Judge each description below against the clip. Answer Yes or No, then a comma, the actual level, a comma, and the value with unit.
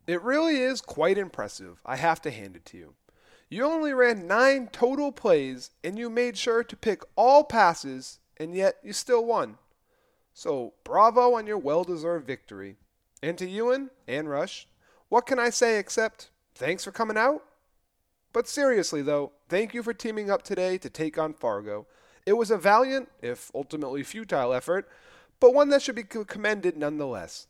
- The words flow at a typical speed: Yes, average, 175 wpm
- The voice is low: No, high, 215 Hz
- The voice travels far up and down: Yes, wide, 8.4 semitones